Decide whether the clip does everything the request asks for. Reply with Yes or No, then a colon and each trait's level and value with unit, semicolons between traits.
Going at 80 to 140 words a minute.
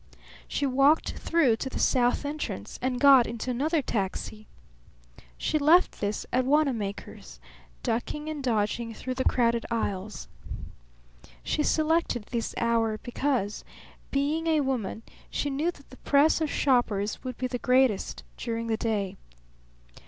Yes: slow, 135 wpm